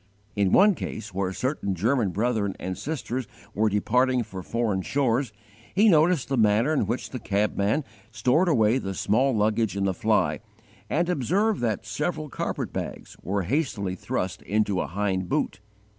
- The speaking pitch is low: Yes, low, 110 Hz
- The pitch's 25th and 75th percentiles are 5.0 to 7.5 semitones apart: Yes, average, 5.3 semitones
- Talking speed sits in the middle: Yes, average, 160 wpm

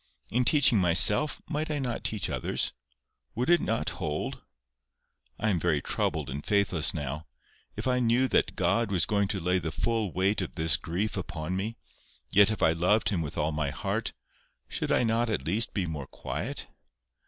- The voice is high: No, very low, 95 Hz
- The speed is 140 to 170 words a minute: No, average, 185 wpm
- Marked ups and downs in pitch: Yes, wide, 5.8 semitones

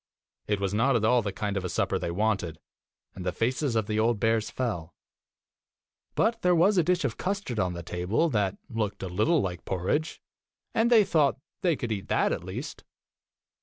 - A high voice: No, low, 110 Hz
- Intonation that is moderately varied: No, wide, 7.7 semitones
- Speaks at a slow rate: No, average, 200 wpm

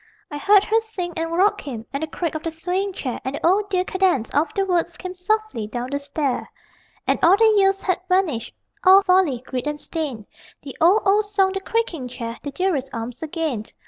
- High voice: Yes, very high, 340 Hz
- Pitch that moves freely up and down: Yes, wide, 5.7 semitones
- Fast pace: Yes, fast, 215 wpm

